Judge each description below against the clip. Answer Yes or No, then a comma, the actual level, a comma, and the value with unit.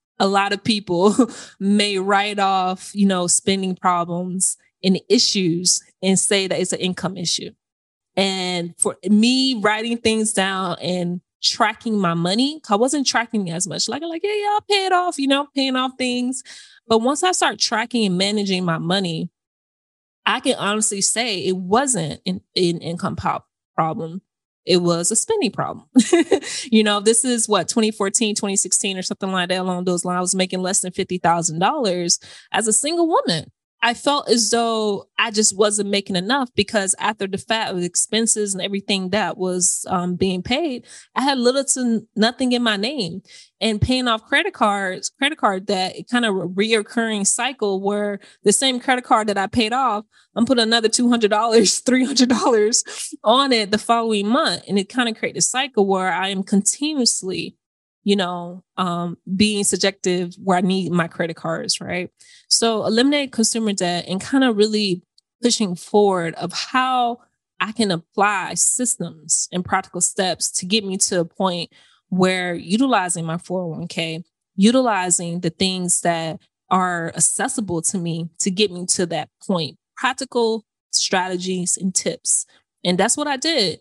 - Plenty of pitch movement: No, average, 4.2 semitones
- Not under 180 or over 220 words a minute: No, average, 170 wpm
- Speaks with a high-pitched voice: Yes, high, 200 Hz